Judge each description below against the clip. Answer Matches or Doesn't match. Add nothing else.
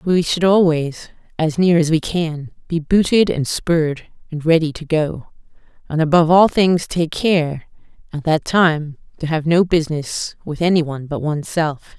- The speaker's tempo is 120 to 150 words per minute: Doesn't match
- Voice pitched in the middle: Matches